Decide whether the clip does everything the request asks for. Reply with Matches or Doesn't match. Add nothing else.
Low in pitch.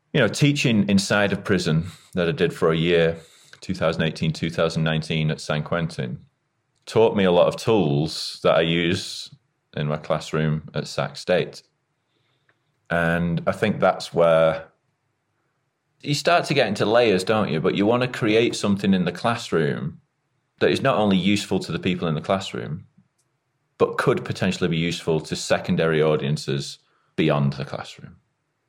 Matches